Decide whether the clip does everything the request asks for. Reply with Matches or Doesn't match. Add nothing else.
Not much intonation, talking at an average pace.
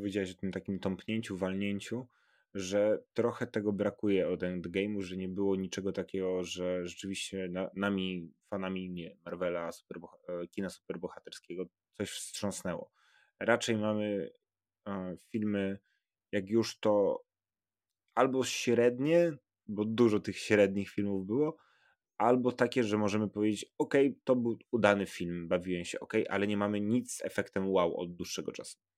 Doesn't match